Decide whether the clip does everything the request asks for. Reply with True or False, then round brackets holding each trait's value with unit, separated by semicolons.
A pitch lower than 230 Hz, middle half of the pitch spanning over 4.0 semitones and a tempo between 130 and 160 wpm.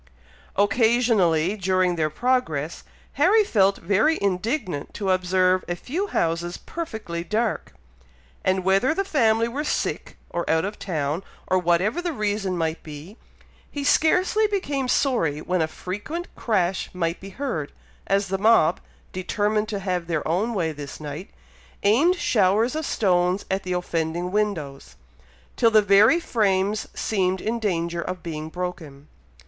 True (190 Hz; 4.7 semitones; 145 wpm)